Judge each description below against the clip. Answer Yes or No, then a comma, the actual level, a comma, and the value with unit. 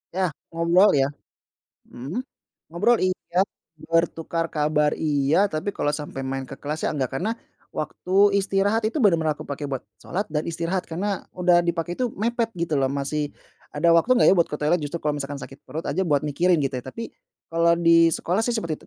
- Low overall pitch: No, medium, 165 Hz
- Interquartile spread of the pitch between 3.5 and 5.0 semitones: Yes, average, 3.9 semitones